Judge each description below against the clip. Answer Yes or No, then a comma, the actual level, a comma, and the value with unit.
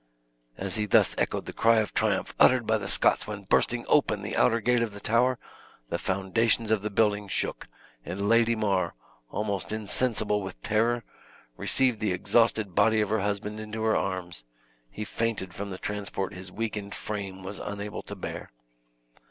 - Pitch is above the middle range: No, low, 105 Hz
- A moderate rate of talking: Yes, average, 175 wpm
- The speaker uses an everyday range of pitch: No, narrow, 2.3 semitones